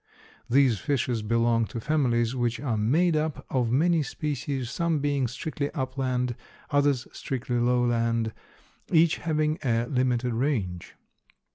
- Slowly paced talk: Yes, slow, 125 wpm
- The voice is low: Yes, low, 130 Hz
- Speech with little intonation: No, average, 3.6 semitones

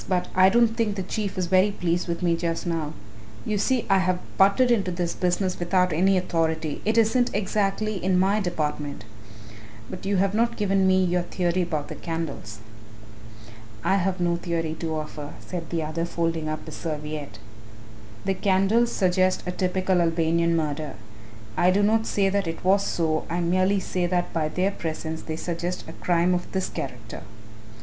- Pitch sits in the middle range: Yes, medium, 180 Hz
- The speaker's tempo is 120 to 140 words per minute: No, average, 180 wpm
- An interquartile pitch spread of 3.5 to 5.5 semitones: No, average, 2.8 semitones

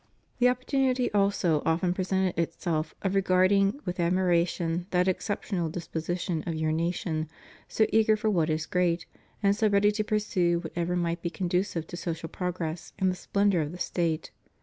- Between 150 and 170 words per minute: Yes, average, 165 wpm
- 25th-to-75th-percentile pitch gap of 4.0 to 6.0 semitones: No, average, 2.9 semitones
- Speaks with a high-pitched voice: No, medium, 180 Hz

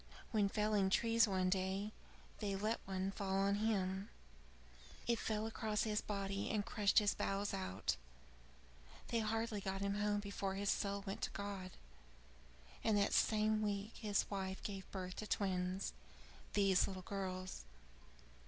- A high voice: Yes, high, 200 Hz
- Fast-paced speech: No, average, 145 wpm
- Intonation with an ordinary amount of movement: No, narrow, 1.7 semitones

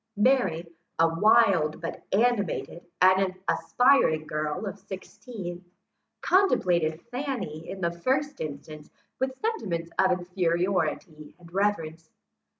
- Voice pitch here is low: No, medium, 185 Hz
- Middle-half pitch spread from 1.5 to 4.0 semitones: No, average, 4.8 semitones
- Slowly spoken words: Yes, slow, 105 wpm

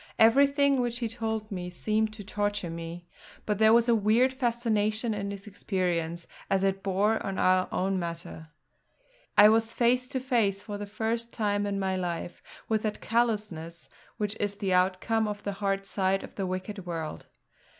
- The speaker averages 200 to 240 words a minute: No, average, 175 wpm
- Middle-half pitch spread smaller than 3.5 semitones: Yes, average, 3.1 semitones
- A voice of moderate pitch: No, high, 205 Hz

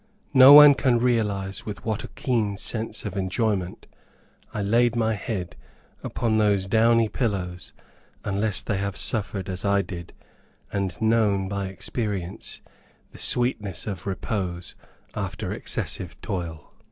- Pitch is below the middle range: Yes, low, 100 Hz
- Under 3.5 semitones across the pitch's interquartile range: Yes, average, 2.9 semitones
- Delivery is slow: Yes, slow, 130 wpm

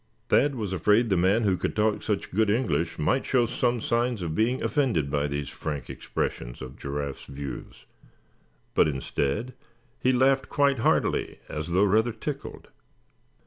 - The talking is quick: No, average, 155 wpm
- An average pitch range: No, wide, 8.1 semitones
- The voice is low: Yes, low, 105 Hz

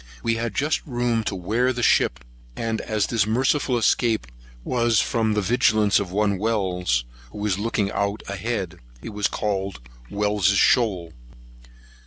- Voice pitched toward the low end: Yes, low, 105 Hz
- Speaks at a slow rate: No, average, 145 wpm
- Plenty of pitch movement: No, average, 2.8 semitones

